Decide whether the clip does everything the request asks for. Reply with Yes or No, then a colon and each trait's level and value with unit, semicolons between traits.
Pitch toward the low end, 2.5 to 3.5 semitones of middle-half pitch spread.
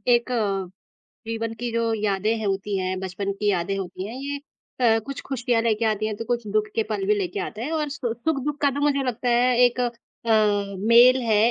No: high, 225 Hz; average, 3.1 semitones